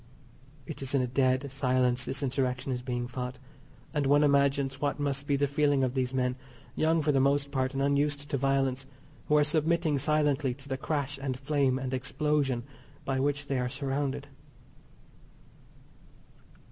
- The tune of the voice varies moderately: No, narrow, 1.8 semitones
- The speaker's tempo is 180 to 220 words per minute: No, average, 170 wpm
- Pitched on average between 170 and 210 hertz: No, low, 135 Hz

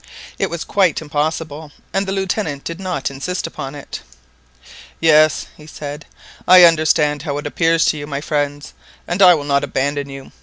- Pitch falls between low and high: Yes, medium, 150 Hz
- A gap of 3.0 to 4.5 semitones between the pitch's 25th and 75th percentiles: No, narrow, 2.6 semitones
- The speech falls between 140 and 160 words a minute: No, average, 175 wpm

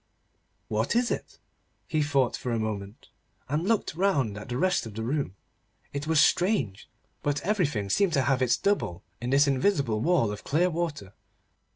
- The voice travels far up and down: Yes, wide, 7.4 semitones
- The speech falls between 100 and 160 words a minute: No, average, 175 wpm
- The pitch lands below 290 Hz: Yes, medium, 140 Hz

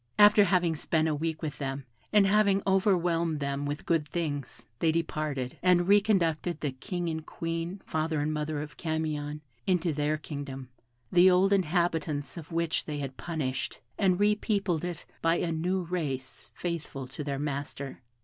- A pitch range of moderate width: Yes, average, 3.3 semitones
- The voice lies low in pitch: No, medium, 160 Hz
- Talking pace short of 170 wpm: Yes, average, 160 wpm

